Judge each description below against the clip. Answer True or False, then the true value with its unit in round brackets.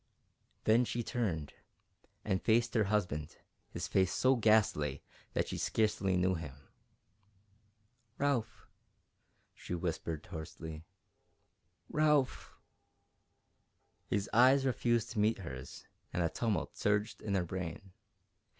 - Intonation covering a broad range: True (5.9 semitones)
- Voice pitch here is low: True (100 Hz)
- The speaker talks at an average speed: False (110 wpm)